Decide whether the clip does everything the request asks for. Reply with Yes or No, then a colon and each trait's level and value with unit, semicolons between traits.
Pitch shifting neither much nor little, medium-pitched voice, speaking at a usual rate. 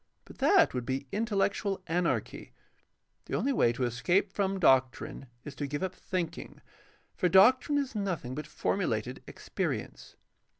No: wide, 7.0 semitones; medium, 175 Hz; average, 145 wpm